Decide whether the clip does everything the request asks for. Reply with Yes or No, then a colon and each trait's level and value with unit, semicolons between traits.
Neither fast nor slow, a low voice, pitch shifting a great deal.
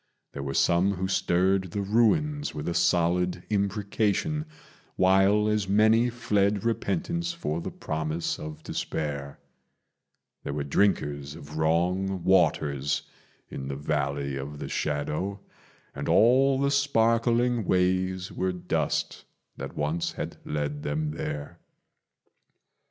No: slow, 120 wpm; very low, 95 Hz; wide, 6.0 semitones